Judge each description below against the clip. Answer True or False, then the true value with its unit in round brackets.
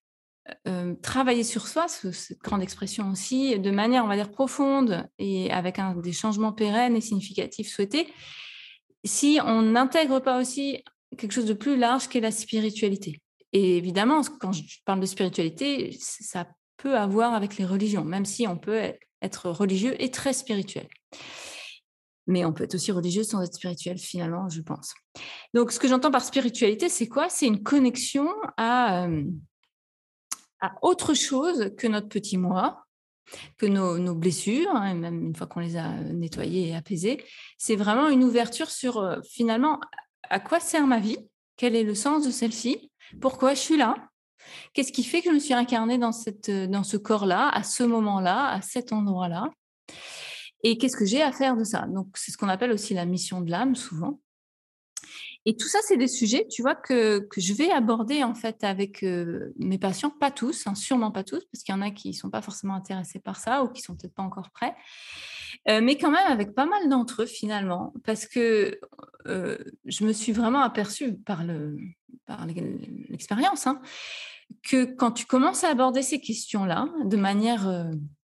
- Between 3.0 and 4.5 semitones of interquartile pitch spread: False (5.2 semitones)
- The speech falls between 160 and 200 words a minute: True (190 wpm)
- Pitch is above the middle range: True (225 Hz)